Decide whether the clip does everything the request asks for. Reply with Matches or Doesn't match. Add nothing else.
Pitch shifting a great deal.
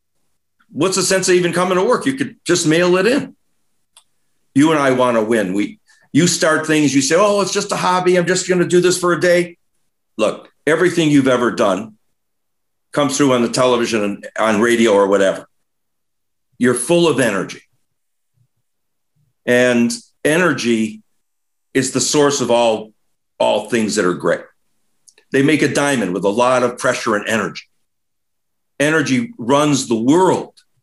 Matches